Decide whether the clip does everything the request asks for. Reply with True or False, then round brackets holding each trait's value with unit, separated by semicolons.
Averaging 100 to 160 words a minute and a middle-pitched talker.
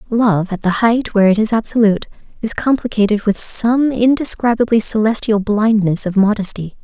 False (150 wpm; 215 Hz)